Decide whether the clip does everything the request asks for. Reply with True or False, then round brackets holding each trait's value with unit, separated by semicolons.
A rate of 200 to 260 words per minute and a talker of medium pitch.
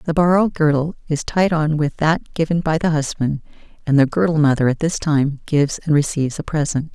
True (205 wpm; 155 Hz)